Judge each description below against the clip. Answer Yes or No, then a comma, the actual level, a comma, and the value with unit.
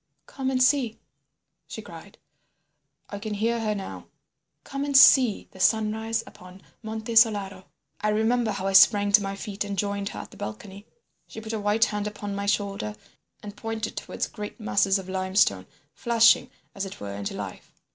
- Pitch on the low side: No, high, 210 Hz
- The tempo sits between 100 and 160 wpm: No, average, 170 wpm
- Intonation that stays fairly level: Yes, narrow, 2.2 semitones